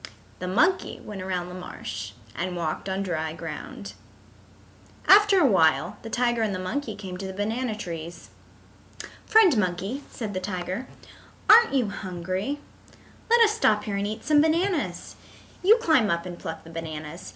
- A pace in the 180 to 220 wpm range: No, average, 160 wpm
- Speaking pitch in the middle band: No, high, 200 Hz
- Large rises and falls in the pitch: Yes, wide, 7.2 semitones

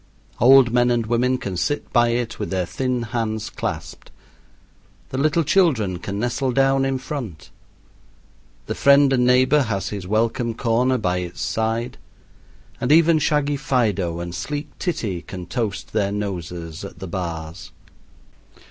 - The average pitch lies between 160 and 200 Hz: No, low, 115 Hz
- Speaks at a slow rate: No, average, 150 wpm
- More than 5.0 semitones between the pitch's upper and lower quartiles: Yes, wide, 5.5 semitones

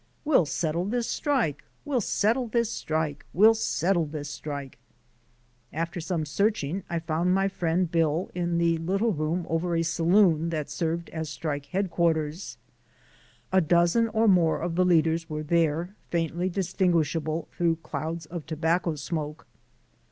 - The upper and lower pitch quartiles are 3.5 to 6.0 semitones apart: No, average, 2.7 semitones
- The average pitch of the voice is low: No, medium, 170 Hz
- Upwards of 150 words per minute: No, average, 145 wpm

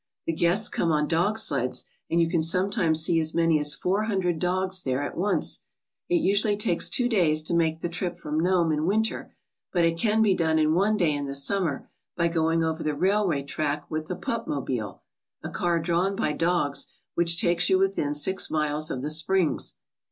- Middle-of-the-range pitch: Yes, medium, 170 Hz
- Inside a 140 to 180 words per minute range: No, fast, 205 wpm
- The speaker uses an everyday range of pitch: Yes, average, 3.4 semitones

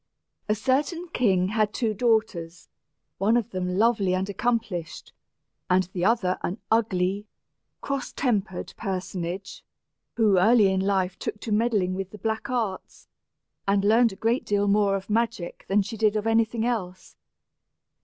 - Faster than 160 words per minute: No, average, 155 wpm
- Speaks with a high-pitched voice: Yes, high, 205 Hz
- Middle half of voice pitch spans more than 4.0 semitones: No, average, 3.2 semitones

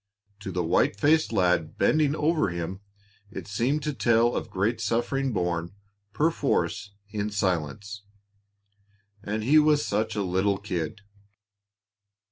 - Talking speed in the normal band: No, slow, 125 wpm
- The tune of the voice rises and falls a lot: Yes, wide, 6.4 semitones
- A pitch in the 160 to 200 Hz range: No, low, 105 Hz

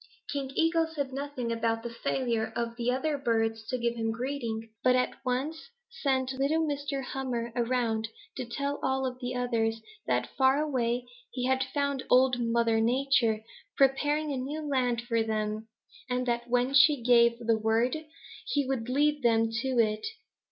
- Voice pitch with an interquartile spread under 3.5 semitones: Yes, average, 2.9 semitones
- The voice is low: No, very high, 250 Hz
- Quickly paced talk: No, average, 165 wpm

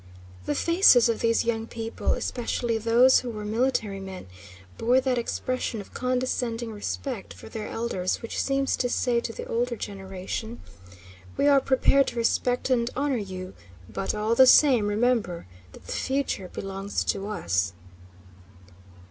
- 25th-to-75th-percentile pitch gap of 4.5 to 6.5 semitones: No, average, 3.6 semitones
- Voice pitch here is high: Yes, high, 230 Hz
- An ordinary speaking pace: Yes, average, 150 wpm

